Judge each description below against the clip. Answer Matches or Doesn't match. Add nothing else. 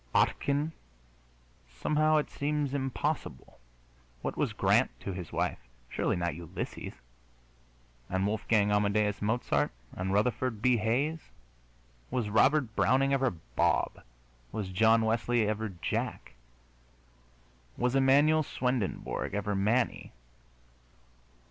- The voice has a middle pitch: Doesn't match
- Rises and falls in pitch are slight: Doesn't match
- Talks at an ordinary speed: Doesn't match